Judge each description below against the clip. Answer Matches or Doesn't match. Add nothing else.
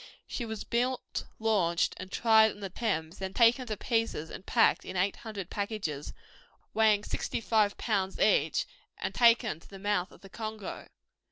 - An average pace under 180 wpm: Matches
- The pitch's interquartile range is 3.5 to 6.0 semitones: Doesn't match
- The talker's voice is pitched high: Matches